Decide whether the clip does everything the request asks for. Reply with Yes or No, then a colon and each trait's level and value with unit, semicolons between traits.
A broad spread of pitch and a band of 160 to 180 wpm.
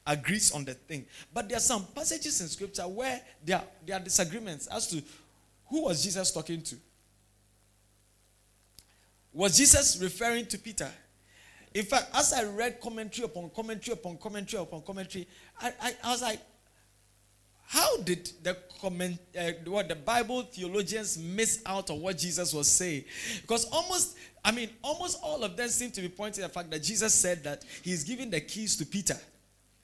Yes: wide, 6.7 semitones; average, 170 wpm